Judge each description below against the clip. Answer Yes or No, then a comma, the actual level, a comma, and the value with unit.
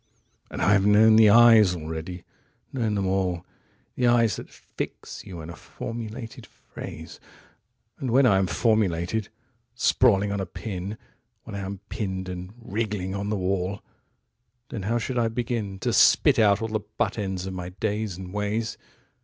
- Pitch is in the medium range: No, low, 105 Hz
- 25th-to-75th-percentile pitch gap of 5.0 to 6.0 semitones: No, average, 3.2 semitones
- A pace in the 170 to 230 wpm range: No, average, 155 wpm